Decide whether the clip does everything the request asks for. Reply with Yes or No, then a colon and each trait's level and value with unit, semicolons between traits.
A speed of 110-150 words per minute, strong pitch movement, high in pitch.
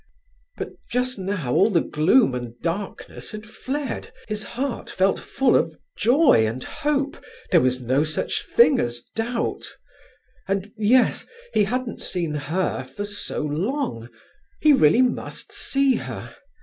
Yes: average, 140 wpm; wide, 8.9 semitones; high, 205 Hz